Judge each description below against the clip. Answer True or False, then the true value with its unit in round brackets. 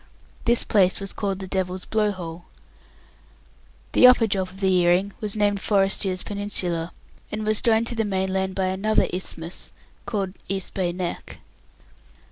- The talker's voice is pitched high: True (195 Hz)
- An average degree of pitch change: False (2.1 semitones)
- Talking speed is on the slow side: False (150 wpm)